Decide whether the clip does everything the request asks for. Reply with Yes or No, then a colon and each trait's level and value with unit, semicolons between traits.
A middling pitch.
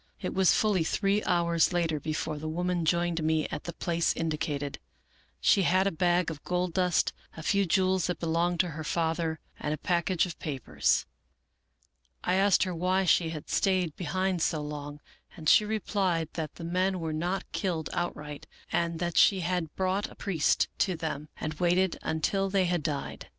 Yes: medium, 170 Hz